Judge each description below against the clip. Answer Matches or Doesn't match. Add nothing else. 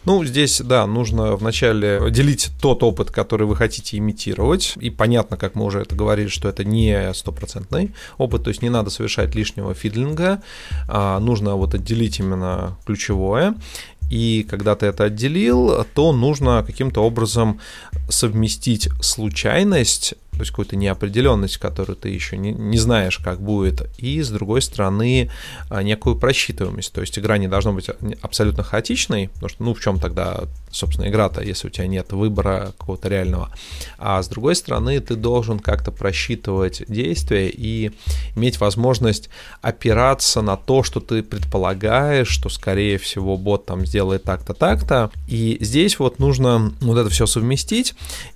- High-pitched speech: Doesn't match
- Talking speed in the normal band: Matches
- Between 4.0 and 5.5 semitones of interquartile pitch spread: Doesn't match